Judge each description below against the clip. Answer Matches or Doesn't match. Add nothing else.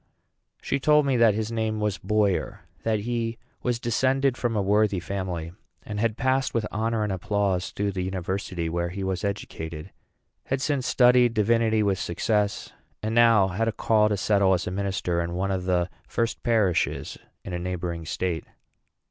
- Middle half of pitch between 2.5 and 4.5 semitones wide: Matches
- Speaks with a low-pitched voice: Matches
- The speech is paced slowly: Doesn't match